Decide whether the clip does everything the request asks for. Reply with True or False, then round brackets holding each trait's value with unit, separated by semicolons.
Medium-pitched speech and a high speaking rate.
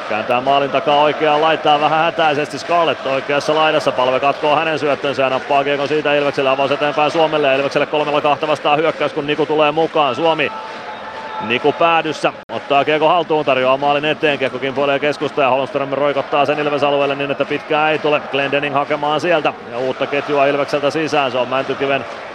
True (145 Hz; 175 wpm)